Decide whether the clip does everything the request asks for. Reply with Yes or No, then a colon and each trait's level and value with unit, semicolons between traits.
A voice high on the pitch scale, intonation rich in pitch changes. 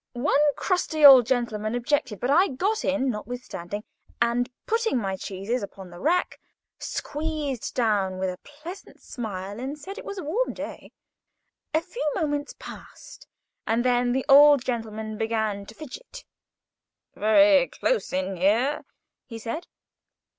Yes: very high, 250 Hz; wide, 5.7 semitones